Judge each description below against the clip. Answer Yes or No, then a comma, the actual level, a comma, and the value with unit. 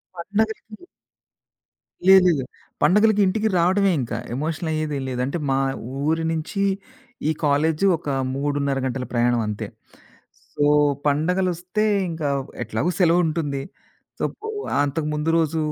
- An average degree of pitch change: Yes, average, 4.2 semitones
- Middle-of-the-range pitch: Yes, medium, 160 Hz